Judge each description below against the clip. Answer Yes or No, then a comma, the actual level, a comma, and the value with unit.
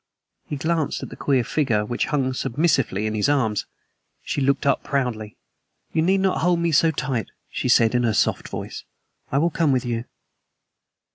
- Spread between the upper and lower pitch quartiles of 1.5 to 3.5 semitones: No, average, 5.0 semitones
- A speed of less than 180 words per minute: No, average, 185 wpm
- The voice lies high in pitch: No, low, 135 Hz